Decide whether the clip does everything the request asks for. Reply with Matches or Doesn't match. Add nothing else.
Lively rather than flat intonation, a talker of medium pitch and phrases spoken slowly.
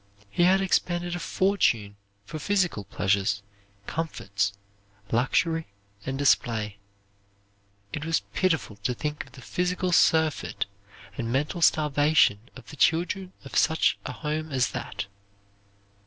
Matches